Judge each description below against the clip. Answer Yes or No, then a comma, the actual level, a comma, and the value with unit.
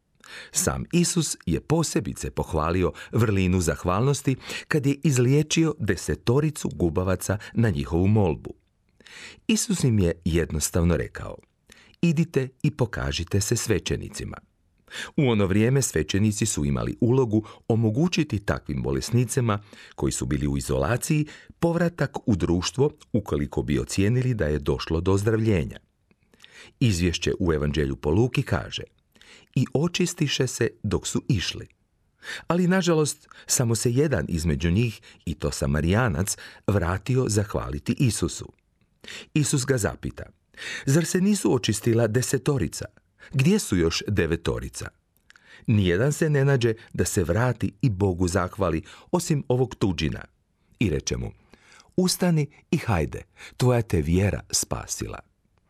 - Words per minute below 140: Yes, average, 120 wpm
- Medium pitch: No, low, 110 Hz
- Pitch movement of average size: No, wide, 8.2 semitones